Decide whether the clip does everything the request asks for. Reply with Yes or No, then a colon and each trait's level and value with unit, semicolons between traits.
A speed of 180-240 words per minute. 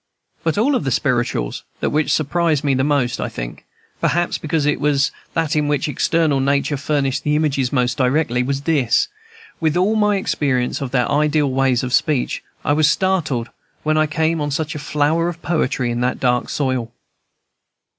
Yes: average, 185 wpm